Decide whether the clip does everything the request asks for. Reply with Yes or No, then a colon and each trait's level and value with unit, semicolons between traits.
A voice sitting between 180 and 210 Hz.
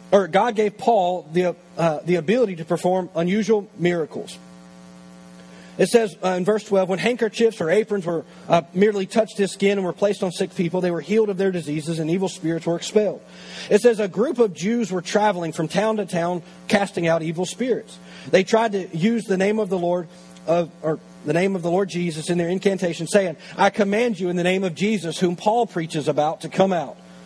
Yes: medium, 185 Hz